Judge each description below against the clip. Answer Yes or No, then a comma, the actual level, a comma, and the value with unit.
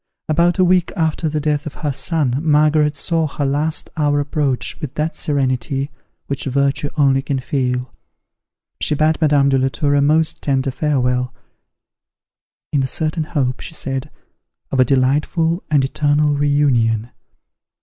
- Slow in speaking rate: No, average, 155 wpm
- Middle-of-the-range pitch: Yes, medium, 145 Hz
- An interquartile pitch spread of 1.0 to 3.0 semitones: Yes, narrow, 2.4 semitones